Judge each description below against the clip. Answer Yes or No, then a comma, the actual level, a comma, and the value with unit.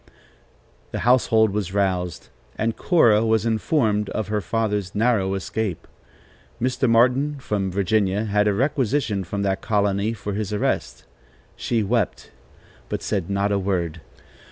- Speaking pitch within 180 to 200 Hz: No, low, 105 Hz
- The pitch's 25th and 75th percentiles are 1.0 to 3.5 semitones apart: Yes, narrow, 2.6 semitones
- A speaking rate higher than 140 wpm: No, slow, 135 wpm